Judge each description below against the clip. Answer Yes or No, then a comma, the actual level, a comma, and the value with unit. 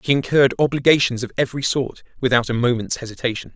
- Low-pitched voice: Yes, low, 125 Hz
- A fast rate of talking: No, average, 170 wpm